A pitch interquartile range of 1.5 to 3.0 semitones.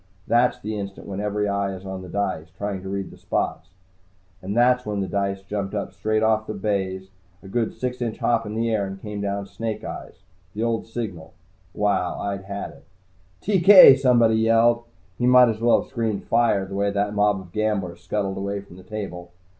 Yes: narrow, 2.6 semitones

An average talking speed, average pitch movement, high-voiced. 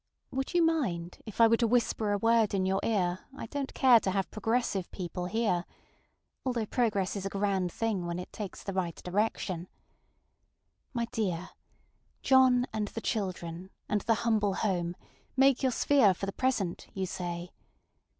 Yes: average, 165 wpm; average, 4.1 semitones; high, 205 Hz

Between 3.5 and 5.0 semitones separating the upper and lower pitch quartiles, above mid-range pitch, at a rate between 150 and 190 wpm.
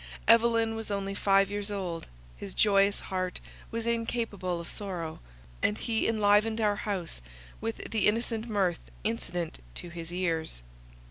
No: average, 3.9 semitones; high, 200 Hz; average, 140 wpm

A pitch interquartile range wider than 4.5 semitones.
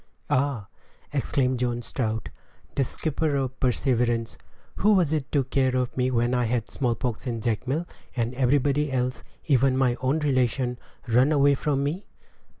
No: narrow, 2.5 semitones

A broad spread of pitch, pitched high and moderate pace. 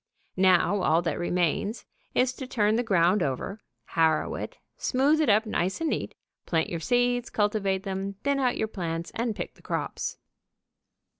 Yes: wide, 5.9 semitones; high, 205 Hz; average, 165 wpm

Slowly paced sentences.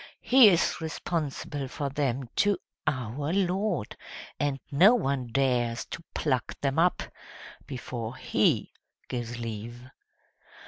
Yes: slow, 110 wpm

